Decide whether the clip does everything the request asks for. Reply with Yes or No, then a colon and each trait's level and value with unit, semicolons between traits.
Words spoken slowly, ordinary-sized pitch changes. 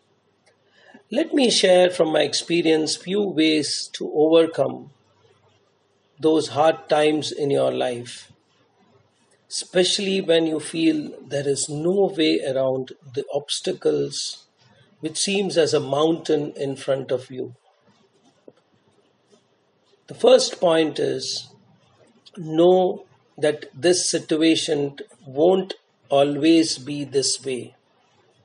Yes: slow, 105 wpm; average, 4.2 semitones